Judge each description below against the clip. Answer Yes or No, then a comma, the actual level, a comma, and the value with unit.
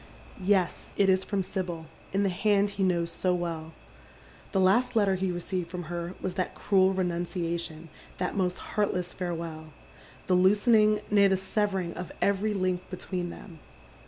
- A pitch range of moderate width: No, narrow, 2.2 semitones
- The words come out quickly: No, average, 160 wpm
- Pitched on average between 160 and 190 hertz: Yes, medium, 185 Hz